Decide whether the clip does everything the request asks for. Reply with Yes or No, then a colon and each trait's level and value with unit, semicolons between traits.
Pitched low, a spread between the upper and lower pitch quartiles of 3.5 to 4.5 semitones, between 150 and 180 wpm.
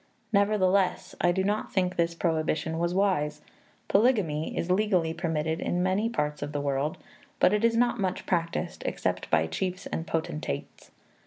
No: medium, 175 Hz; average, 3.8 semitones; average, 155 wpm